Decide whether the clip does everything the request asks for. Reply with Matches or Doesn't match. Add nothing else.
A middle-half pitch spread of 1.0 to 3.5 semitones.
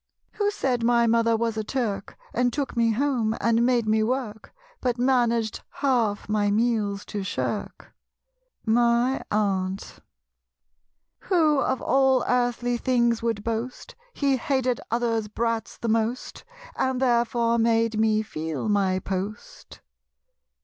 Matches